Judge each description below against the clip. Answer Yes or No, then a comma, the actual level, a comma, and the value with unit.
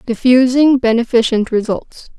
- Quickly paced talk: No, slow, 80 wpm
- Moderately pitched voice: No, high, 240 Hz